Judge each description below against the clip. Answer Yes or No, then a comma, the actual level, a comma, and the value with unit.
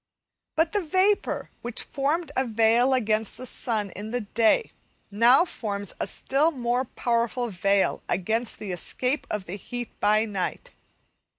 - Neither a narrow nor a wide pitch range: Yes, average, 3.9 semitones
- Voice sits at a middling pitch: No, high, 235 Hz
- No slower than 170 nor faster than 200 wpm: No, average, 150 wpm